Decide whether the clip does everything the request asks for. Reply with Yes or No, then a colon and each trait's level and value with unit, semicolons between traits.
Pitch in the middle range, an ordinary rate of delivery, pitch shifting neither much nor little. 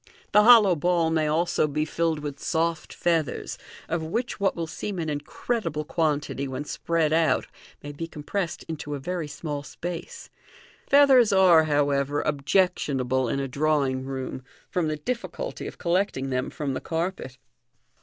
Yes: medium, 155 Hz; average, 165 wpm; average, 3.4 semitones